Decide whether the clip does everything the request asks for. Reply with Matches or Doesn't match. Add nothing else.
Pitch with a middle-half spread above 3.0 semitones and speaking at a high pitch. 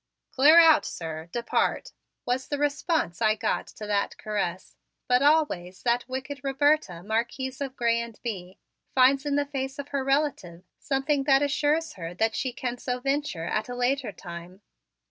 Matches